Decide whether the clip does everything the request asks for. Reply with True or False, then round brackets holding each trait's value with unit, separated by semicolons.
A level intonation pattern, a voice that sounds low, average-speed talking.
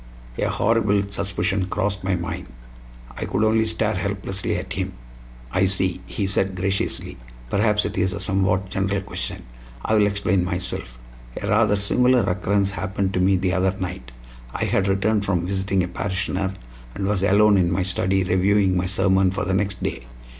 True (1.4 semitones; 95 Hz; 175 wpm)